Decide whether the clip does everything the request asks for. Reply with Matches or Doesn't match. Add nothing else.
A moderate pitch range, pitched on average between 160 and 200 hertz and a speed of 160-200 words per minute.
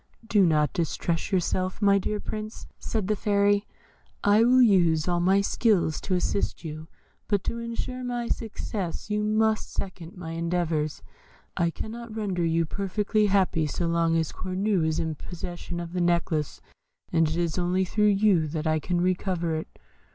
Matches